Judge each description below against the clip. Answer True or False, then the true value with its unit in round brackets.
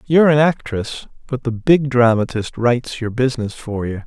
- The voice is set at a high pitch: False (125 Hz)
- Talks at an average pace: True (175 wpm)